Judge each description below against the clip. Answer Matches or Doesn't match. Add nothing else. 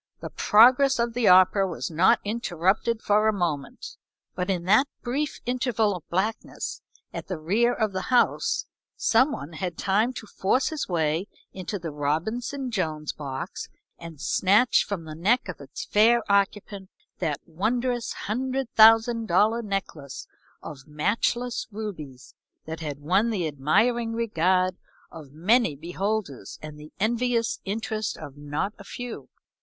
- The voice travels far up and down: Matches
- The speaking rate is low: Doesn't match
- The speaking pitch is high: Matches